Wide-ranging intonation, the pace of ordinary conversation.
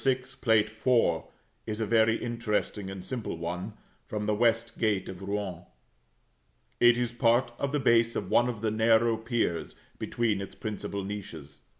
No: average, 2.8 semitones; average, 165 wpm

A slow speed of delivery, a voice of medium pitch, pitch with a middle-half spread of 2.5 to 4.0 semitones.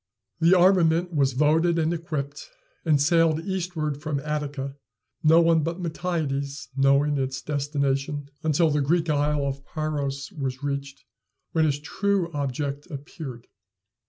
Yes: slow, 130 wpm; medium, 150 Hz; average, 2.9 semitones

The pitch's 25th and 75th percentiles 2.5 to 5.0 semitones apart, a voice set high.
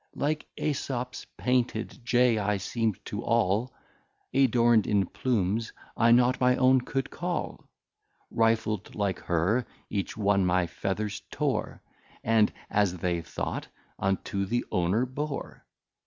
No: average, 4.3 semitones; low, 110 Hz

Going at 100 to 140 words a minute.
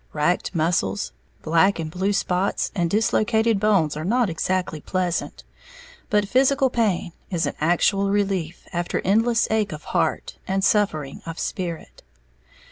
Yes: slow, 135 wpm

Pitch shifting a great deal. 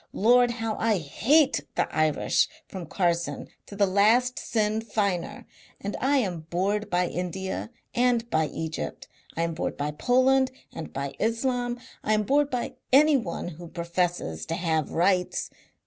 Yes: wide, 6.2 semitones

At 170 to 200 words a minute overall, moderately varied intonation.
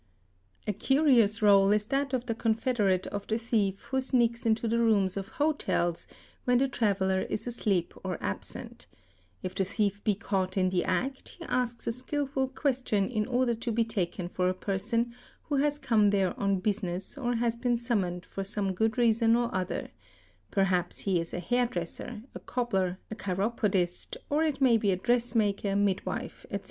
Yes: average, 180 wpm; average, 4.0 semitones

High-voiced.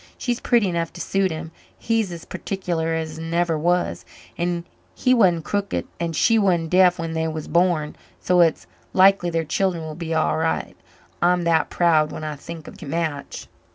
No: medium, 170 Hz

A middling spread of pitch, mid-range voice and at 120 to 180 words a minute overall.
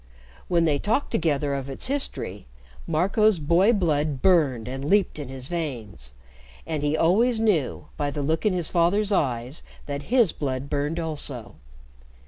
Yes: average, 4.8 semitones; medium, 155 Hz; average, 155 wpm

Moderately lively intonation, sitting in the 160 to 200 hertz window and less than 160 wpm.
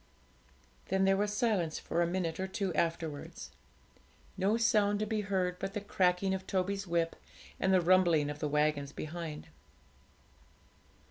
Yes: average, 3.1 semitones; medium, 185 Hz; average, 150 wpm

